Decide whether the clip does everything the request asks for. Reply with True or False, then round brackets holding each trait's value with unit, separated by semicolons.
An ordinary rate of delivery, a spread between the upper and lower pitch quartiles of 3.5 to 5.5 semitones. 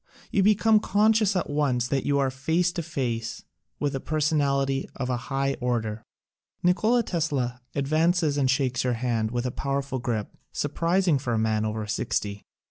True (170 wpm; 5.0 semitones)